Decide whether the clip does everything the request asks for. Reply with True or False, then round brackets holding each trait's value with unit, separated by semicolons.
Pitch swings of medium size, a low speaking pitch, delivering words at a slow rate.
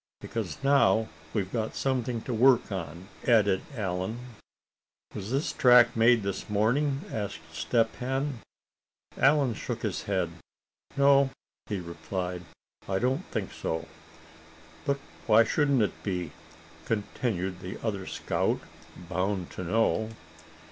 True (5.0 semitones; 110 Hz; 120 wpm)